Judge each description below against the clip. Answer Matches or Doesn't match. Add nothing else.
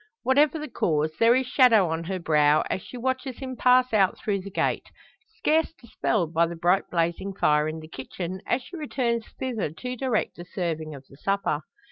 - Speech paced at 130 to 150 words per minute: Doesn't match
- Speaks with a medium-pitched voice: Doesn't match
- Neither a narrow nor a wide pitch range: Doesn't match